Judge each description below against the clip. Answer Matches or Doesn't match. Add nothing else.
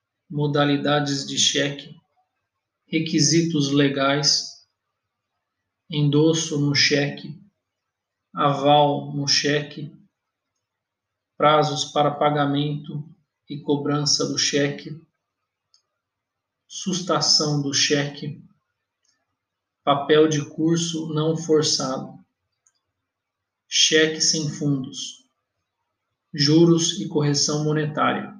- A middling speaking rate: Doesn't match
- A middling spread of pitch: Doesn't match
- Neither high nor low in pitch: Matches